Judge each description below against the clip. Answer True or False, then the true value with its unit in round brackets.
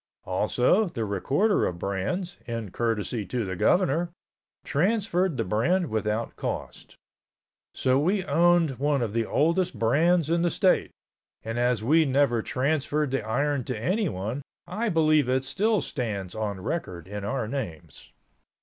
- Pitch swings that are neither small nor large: False (7.5 semitones)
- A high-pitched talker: False (135 Hz)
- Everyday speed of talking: True (145 wpm)